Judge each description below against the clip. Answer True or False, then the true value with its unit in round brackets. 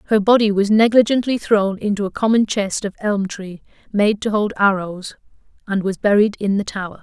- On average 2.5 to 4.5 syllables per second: False (5.3 syllables/s)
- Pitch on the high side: True (205 Hz)